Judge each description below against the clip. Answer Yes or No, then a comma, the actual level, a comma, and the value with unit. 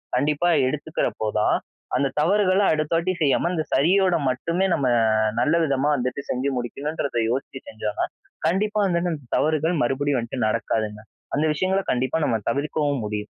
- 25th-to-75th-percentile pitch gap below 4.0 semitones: No, average, 5.0 semitones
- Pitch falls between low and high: Yes, medium, 145 Hz